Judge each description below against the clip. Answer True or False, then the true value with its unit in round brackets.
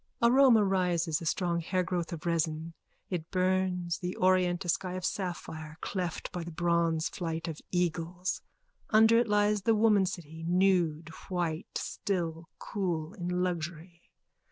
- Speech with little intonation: True (2.1 semitones)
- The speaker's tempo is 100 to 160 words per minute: True (135 wpm)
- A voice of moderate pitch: True (175 Hz)